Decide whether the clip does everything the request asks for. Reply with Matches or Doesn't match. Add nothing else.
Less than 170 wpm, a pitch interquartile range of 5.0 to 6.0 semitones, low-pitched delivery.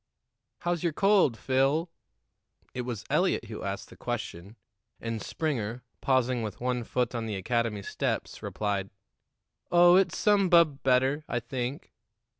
Matches